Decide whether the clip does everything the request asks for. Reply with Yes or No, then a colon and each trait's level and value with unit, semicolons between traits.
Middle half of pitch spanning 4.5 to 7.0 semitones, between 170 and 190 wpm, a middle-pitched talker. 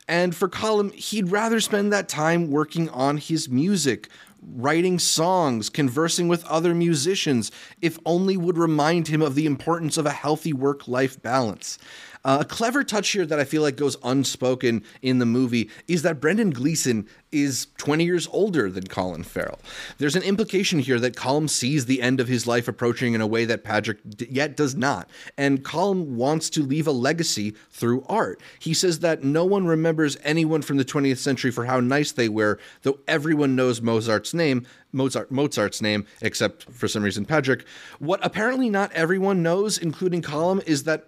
Yes: average, 5.0 semitones; average, 185 wpm; medium, 150 Hz